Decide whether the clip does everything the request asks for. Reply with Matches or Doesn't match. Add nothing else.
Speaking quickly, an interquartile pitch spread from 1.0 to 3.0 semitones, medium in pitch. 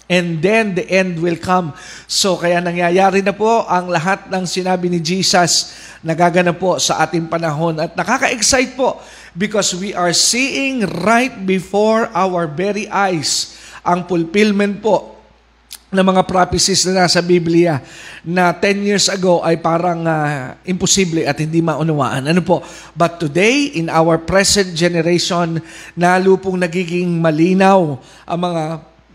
Doesn't match